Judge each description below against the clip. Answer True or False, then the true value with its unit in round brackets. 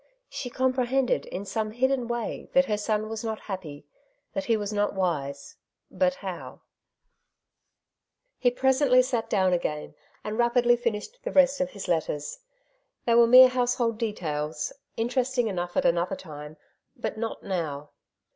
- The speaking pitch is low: False (225 Hz)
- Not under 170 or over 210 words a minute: False (150 wpm)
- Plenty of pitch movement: True (5.7 semitones)